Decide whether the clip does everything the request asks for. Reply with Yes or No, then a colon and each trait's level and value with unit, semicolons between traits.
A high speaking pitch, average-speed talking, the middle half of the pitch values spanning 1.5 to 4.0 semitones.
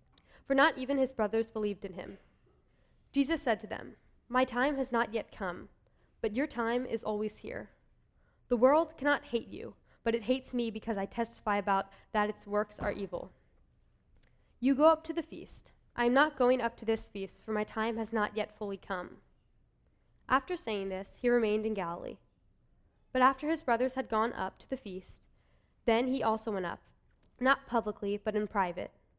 Yes: high, 225 Hz; average, 185 wpm; average, 3.6 semitones